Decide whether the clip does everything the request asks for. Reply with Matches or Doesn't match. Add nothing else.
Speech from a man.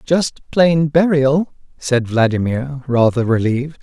Matches